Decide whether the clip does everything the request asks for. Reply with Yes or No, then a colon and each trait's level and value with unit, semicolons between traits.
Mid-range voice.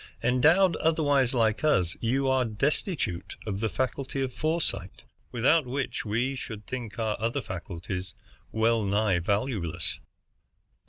No: low, 115 Hz